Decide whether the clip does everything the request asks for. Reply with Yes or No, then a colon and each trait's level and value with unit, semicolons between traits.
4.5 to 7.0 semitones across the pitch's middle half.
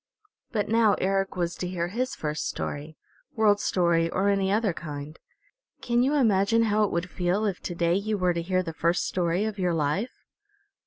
No: average, 3.7 semitones